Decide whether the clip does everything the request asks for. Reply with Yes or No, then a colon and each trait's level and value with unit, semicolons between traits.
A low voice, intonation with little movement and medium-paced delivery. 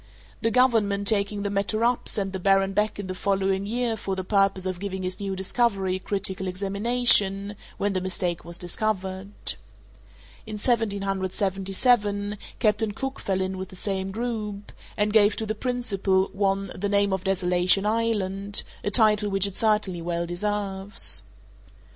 No: high, 200 Hz; narrow, 1.7 semitones; average, 160 wpm